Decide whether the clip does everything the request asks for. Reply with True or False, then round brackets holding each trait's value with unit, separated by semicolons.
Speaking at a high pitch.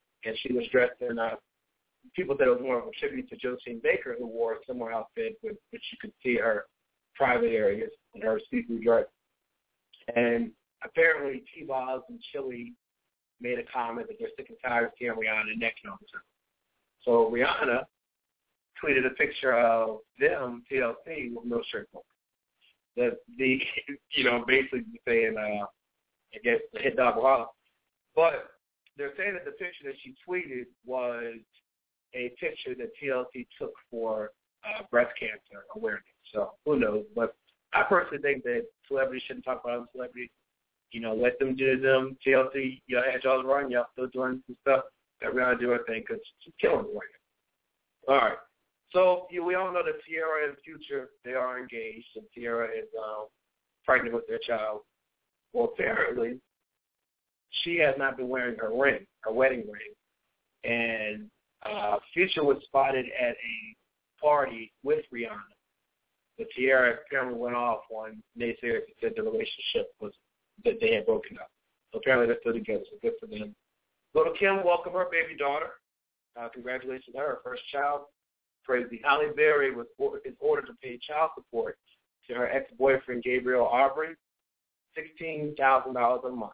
False (135 Hz)